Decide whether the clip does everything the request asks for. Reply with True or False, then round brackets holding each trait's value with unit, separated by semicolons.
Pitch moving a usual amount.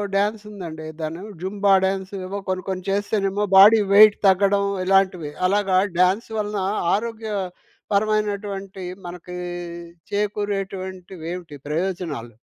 False (2.0 semitones)